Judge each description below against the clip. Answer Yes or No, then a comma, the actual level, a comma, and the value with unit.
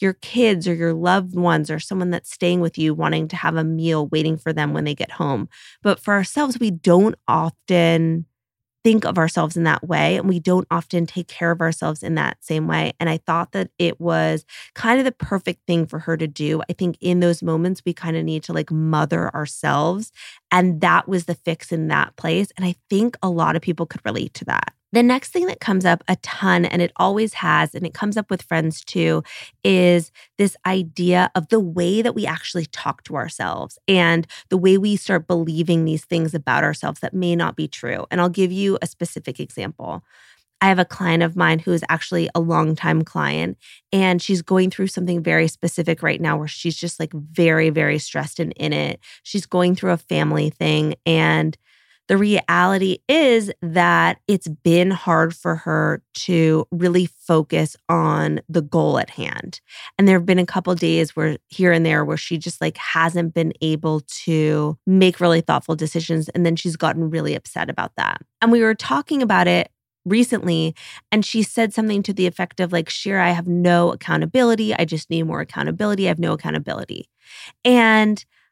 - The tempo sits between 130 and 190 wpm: No, fast, 205 wpm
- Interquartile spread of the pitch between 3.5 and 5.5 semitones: No, average, 2.7 semitones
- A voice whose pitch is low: No, medium, 170 Hz